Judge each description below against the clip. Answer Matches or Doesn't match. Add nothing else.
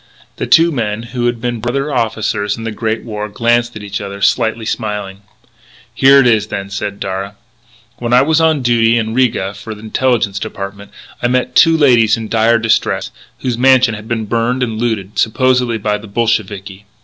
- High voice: Doesn't match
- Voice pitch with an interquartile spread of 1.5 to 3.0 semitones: Matches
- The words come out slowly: Doesn't match